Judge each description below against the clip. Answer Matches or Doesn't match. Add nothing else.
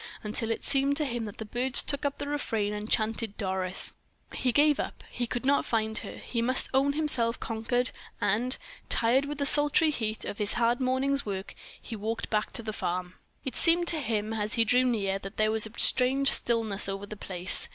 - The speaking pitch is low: Doesn't match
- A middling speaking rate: Doesn't match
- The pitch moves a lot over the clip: Doesn't match